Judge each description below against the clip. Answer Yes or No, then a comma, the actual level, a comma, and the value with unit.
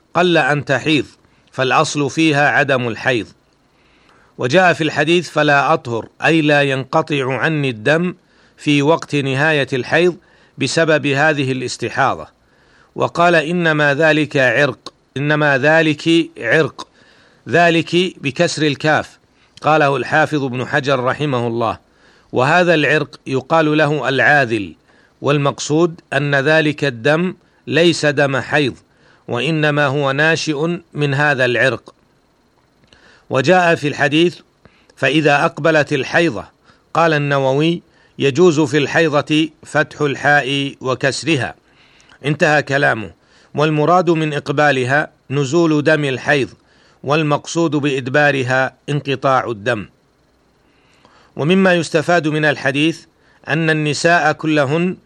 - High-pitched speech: No, medium, 150 Hz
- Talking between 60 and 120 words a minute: Yes, average, 100 wpm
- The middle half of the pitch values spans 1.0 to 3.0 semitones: Yes, average, 2.7 semitones